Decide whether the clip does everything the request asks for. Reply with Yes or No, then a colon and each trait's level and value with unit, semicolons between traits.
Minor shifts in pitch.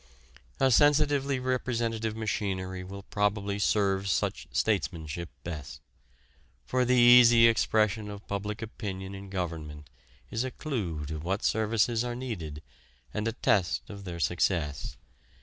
No: average, 4.1 semitones